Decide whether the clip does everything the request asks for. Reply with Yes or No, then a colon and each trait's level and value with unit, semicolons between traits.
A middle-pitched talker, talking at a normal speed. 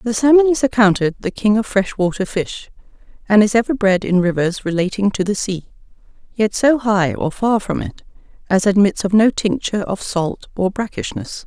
No: high, 210 Hz; average, 185 wpm